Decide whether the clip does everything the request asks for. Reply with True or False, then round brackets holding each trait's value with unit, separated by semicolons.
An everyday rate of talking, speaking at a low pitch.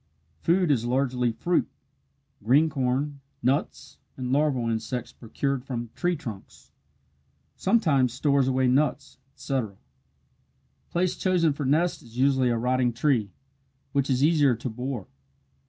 False (125 wpm; 130 Hz)